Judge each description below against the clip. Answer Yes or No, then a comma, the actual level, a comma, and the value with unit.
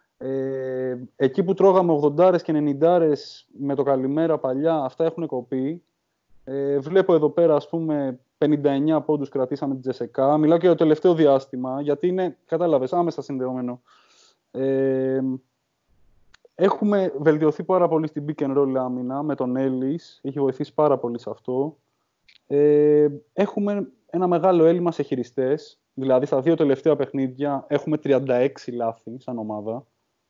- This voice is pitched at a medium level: Yes, medium, 145 Hz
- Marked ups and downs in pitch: No, average, 3.7 semitones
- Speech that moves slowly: No, average, 140 wpm